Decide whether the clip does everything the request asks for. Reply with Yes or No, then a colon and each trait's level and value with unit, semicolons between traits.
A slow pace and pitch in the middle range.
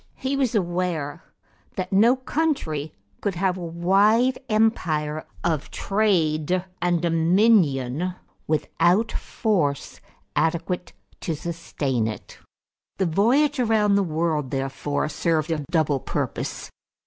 Yes: slow, 110 wpm; medium, 175 Hz